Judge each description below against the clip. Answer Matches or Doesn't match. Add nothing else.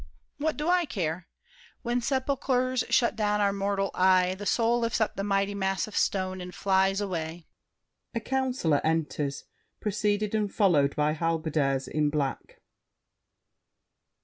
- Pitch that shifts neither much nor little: Doesn't match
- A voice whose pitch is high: Matches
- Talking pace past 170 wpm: Doesn't match